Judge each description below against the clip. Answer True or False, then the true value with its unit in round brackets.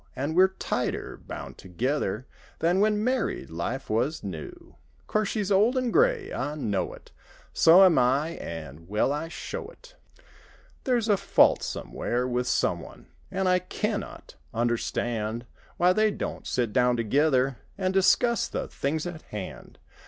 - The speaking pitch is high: False (150 Hz)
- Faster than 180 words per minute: False (145 wpm)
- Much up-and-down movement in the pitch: True (8.5 semitones)